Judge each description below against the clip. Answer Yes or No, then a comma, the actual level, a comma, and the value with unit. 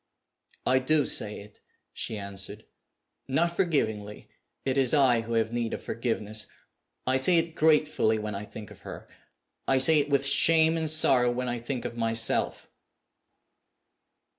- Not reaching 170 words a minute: Yes, average, 155 wpm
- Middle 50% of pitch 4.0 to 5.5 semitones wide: Yes, average, 5.1 semitones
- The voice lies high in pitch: No, low, 125 Hz